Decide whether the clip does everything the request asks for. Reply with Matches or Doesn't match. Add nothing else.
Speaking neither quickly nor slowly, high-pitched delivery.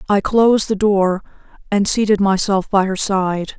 Matches